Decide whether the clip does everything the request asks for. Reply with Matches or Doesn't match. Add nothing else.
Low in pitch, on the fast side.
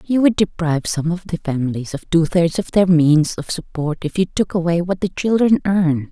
Doesn't match